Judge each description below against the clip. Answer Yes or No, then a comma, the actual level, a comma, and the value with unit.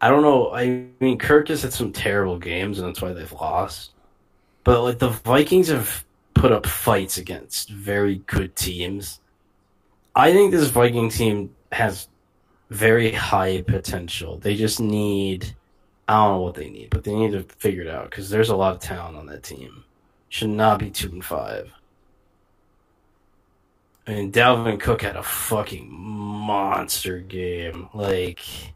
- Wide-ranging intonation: No, average, 3.2 semitones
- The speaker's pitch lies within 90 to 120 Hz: Yes, low, 100 Hz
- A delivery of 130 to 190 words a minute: Yes, average, 165 wpm